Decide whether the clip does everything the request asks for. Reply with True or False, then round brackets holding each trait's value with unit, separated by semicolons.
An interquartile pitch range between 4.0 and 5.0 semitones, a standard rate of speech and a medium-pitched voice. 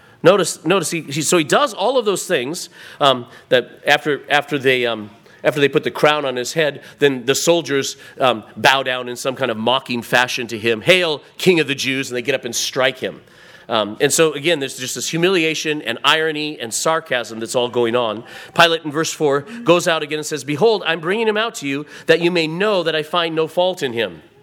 False (4.6 semitones; 230 wpm; 150 Hz)